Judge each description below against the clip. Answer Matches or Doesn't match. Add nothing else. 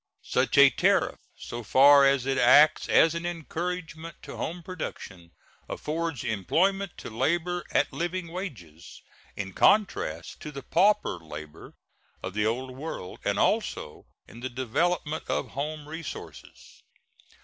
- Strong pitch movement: Matches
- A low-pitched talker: Doesn't match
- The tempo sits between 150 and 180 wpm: Doesn't match